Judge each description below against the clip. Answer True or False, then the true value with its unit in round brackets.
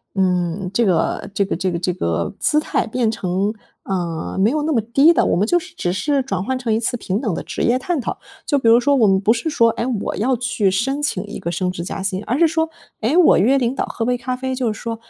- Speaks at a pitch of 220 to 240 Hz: True (230 Hz)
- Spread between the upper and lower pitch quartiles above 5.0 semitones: True (5.5 semitones)